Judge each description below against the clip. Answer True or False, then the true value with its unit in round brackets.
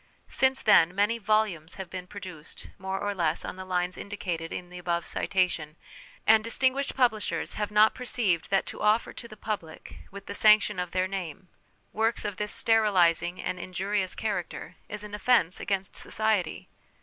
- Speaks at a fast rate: False (170 wpm)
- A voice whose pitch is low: False (195 Hz)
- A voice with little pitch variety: False (3.1 semitones)